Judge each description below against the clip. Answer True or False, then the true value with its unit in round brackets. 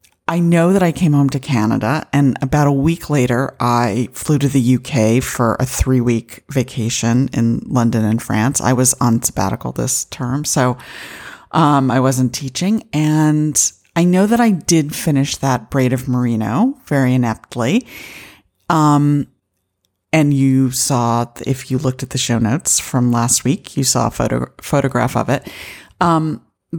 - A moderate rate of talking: True (165 wpm)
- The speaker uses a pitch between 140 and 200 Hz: False (130 Hz)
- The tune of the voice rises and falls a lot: False (3.7 semitones)